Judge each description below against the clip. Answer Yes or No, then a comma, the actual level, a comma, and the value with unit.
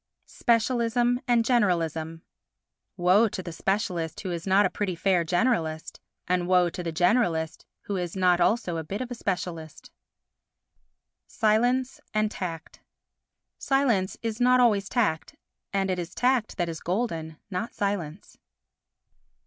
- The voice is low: No, high, 190 Hz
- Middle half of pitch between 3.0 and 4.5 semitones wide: No, average, 5.1 semitones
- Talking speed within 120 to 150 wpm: Yes, average, 140 wpm